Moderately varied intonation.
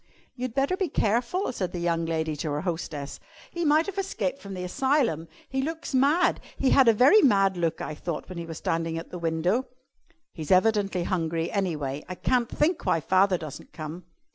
No: wide, 8.2 semitones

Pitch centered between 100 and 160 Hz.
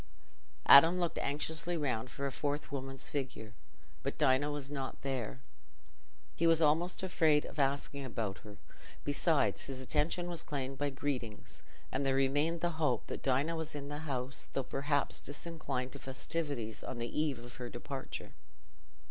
Yes: medium, 140 Hz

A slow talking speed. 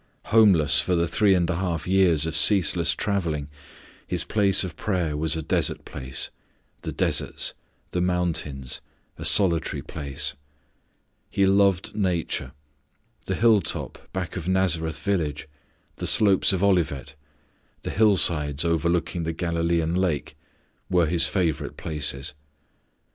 Yes: slow, 125 wpm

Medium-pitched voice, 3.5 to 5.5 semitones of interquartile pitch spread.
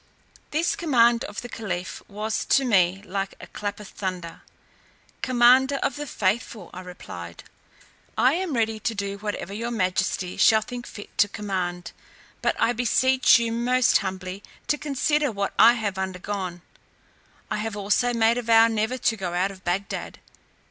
No: high, 215 Hz; average, 4.1 semitones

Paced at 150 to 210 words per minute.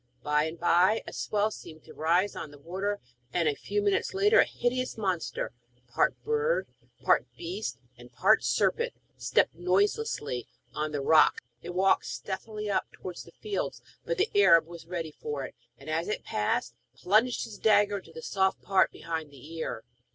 Yes: average, 180 wpm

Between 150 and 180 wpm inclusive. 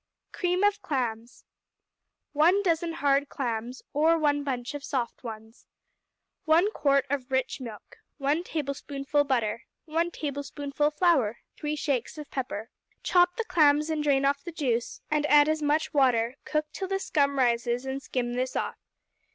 Yes: average, 155 wpm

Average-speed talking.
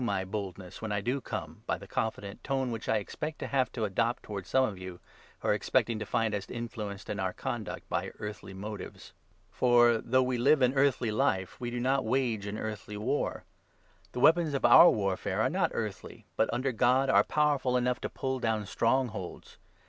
No: fast, 210 wpm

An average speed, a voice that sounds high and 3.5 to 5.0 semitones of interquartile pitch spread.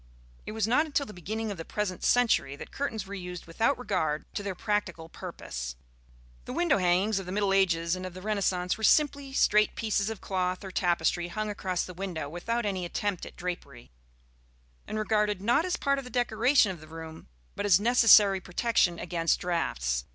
Yes: average, 195 wpm; high, 195 Hz; average, 4.0 semitones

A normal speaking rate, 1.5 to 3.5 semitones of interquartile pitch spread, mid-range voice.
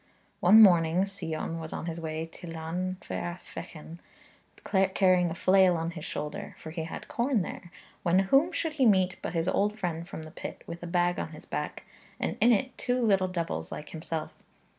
Yes: average, 190 wpm; average, 3.0 semitones; medium, 175 Hz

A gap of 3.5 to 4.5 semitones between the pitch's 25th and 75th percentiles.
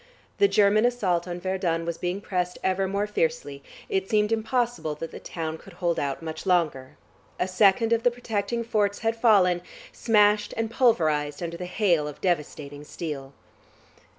No: average, 5.1 semitones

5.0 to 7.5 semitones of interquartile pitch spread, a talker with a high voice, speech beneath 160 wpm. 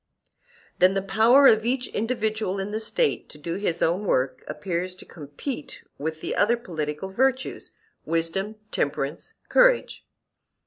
Yes: wide, 5.6 semitones; high, 195 Hz; average, 140 wpm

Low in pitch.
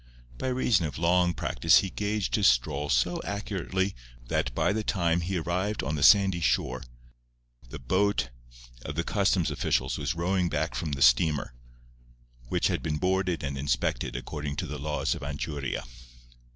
Yes: very low, 85 Hz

